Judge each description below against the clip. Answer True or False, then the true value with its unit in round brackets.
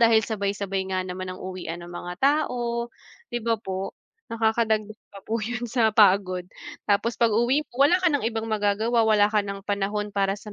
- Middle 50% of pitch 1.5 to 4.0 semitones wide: True (2.8 semitones)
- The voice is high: True (215 Hz)